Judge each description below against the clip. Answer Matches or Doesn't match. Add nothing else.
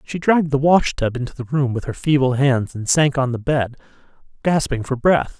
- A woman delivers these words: Doesn't match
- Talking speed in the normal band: Doesn't match